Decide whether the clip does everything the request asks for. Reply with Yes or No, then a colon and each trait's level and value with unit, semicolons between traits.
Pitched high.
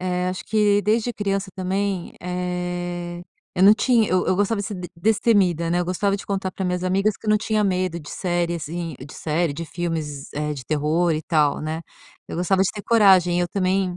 No: medium, 180 Hz